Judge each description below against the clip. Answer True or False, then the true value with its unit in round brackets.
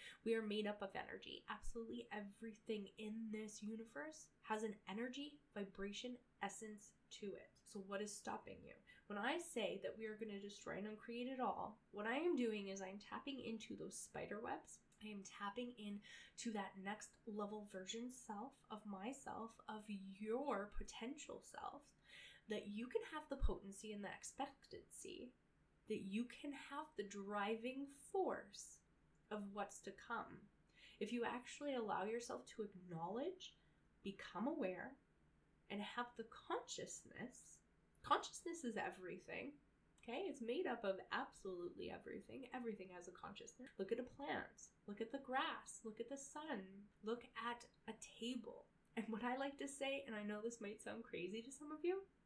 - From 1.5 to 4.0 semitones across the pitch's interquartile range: True (3.7 semitones)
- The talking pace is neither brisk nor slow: True (165 wpm)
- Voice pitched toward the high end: True (225 Hz)